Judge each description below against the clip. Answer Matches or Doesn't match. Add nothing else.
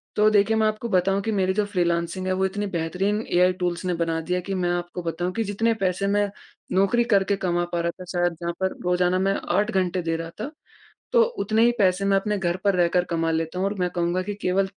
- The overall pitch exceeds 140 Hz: Matches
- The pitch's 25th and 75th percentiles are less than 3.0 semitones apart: Matches